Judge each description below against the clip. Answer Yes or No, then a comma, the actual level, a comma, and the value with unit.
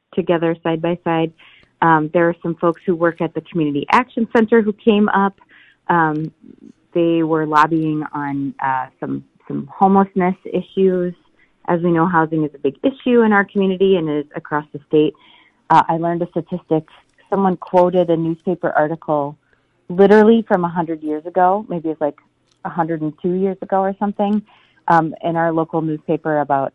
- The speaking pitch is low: No, medium, 170 Hz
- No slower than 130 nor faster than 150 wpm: No, average, 175 wpm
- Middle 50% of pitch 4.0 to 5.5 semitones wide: No, average, 3.5 semitones